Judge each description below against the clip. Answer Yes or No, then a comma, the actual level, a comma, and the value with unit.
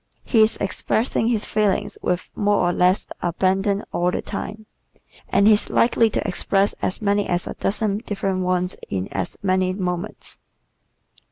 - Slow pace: No, average, 160 wpm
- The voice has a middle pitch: No, high, 195 Hz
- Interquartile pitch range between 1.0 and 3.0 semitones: Yes, narrow, 2.5 semitones